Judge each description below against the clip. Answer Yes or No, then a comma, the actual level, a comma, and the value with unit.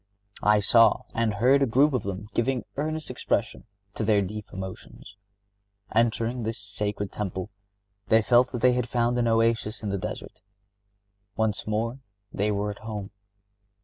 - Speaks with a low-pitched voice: Yes, low, 110 Hz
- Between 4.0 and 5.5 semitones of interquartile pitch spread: No, average, 2.7 semitones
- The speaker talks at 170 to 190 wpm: No, average, 155 wpm